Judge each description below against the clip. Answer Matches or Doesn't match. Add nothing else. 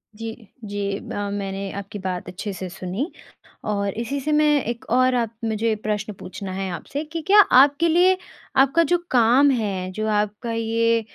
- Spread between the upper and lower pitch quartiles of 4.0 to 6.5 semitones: Matches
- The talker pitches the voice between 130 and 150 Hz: Doesn't match